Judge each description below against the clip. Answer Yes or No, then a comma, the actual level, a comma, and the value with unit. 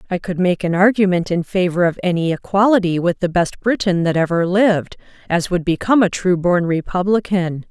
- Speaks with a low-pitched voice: No, medium, 180 Hz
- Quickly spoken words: No, average, 180 wpm